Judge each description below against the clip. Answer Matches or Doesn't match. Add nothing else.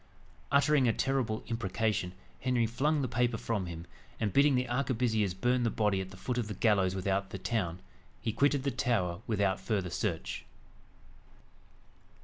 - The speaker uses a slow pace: Doesn't match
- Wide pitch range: Doesn't match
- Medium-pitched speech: Doesn't match